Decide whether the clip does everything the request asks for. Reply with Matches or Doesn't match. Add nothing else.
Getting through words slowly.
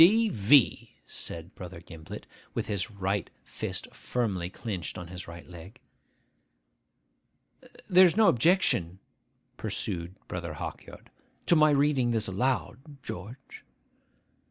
Matches